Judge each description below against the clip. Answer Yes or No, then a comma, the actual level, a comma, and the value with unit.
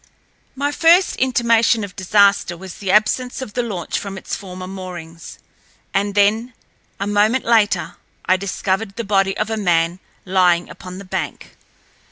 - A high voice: Yes, high, 200 Hz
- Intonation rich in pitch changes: No, average, 3.2 semitones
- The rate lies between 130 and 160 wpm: Yes, average, 150 wpm